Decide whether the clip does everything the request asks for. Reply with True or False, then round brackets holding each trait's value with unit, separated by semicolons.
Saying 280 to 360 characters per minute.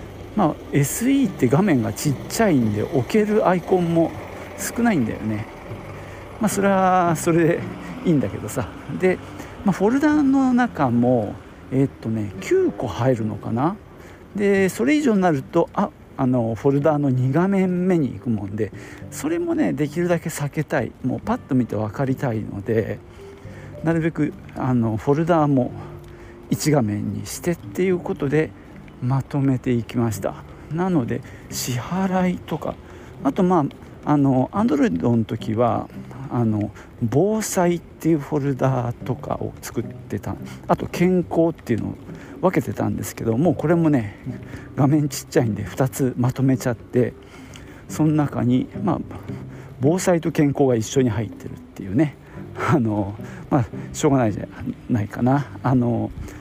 True (285 characters per minute)